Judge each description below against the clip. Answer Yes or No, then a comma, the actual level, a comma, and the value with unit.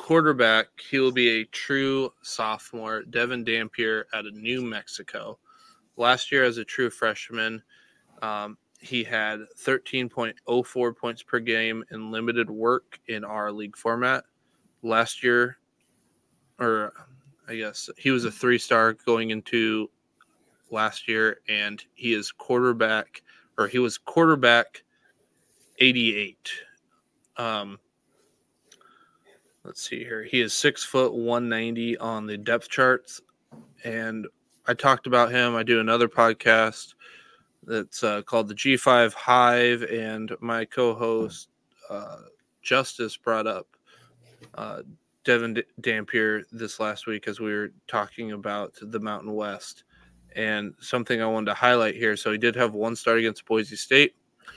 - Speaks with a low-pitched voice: Yes, low, 115 Hz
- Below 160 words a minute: Yes, slow, 135 wpm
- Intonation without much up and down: Yes, narrow, 1.9 semitones